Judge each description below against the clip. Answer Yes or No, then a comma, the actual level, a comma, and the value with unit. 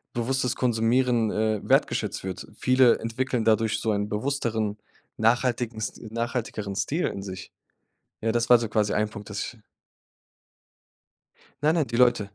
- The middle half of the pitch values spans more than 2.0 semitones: Yes, narrow, 2.6 semitones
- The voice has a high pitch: No, low, 115 Hz